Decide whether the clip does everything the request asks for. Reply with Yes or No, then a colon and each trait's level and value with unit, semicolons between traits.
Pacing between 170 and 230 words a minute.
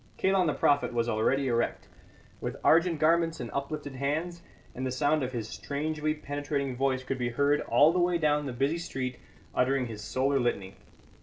Yes: average, 180 wpm